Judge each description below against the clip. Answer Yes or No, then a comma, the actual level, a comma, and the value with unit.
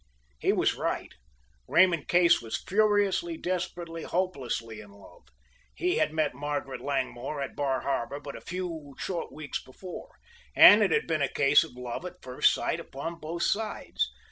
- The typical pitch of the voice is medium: Yes, medium, 155 Hz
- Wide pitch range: No, average, 5.0 semitones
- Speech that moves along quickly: No, average, 165 wpm